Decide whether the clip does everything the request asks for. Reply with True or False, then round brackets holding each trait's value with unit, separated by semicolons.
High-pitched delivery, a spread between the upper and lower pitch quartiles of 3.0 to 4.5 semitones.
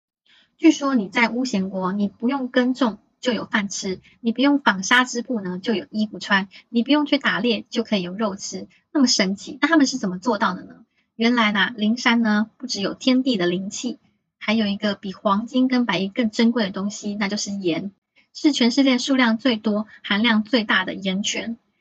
True (225 Hz; 3.6 semitones)